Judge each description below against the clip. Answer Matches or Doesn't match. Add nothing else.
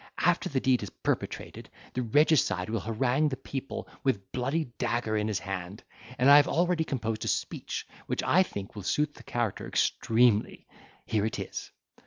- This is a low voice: Matches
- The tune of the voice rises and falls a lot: Doesn't match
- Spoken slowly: Doesn't match